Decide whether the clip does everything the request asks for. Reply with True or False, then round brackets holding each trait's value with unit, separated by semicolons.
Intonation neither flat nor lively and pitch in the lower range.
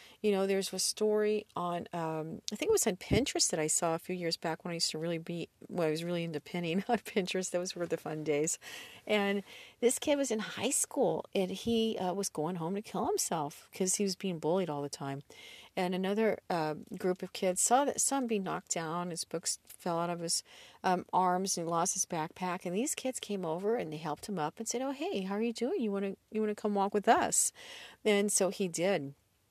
False (4.0 semitones; 185 Hz)